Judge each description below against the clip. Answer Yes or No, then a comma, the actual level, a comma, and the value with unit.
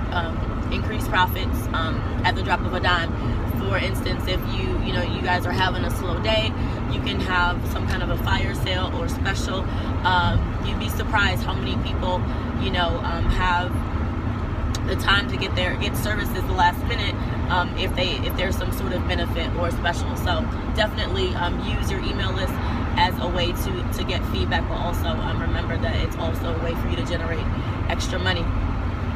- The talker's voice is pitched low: Yes, very low, 95 Hz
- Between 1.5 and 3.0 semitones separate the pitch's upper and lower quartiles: No, average, 3.8 semitones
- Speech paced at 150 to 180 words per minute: No, average, 195 wpm